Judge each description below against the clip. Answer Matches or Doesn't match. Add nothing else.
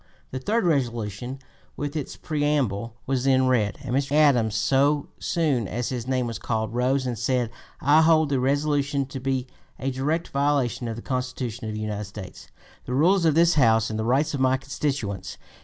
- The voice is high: Doesn't match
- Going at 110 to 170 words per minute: Doesn't match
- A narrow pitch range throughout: Doesn't match